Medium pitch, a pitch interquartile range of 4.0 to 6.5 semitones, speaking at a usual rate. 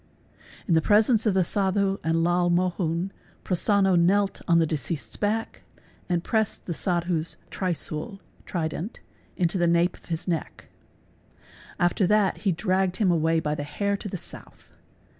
No: medium, 180 Hz; average, 2.9 semitones; average, 160 wpm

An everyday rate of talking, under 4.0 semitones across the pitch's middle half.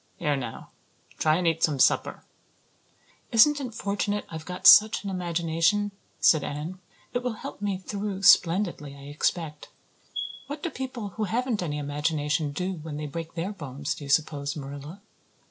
No: average, 160 wpm; wide, 5.6 semitones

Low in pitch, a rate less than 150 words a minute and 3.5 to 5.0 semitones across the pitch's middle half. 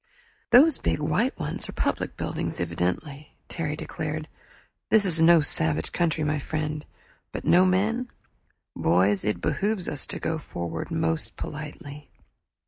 No: medium, 155 Hz; slow, 135 wpm; average, 4.0 semitones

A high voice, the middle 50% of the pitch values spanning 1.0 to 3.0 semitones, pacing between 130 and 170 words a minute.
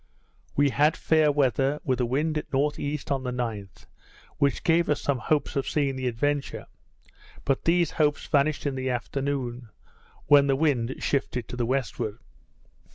No: medium, 140 Hz; average, 2.7 semitones; average, 160 wpm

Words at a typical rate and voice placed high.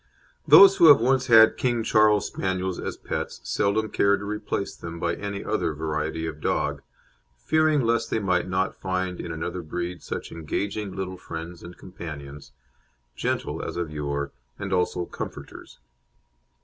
No: average, 155 wpm; very low, 95 Hz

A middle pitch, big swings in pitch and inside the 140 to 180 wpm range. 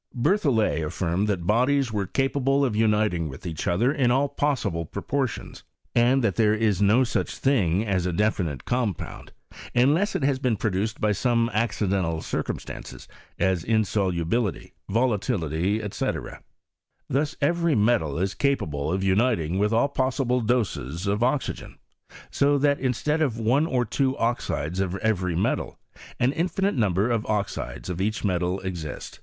No: low, 110 Hz; wide, 5.7 semitones; average, 150 wpm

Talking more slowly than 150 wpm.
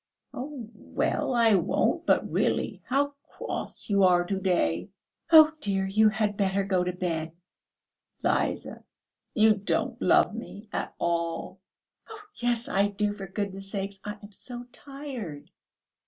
Yes: average, 140 wpm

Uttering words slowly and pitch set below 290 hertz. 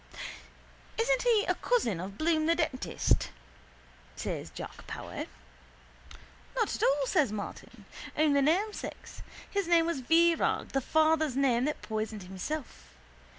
No: slow, 125 wpm; very high, 310 Hz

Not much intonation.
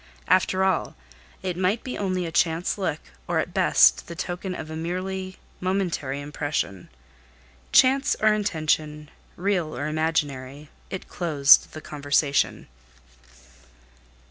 No: average, 3.8 semitones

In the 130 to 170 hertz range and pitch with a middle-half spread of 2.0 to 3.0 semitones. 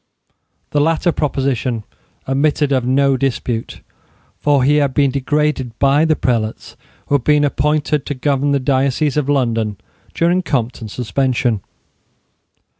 Yes: medium, 140 Hz; average, 2.7 semitones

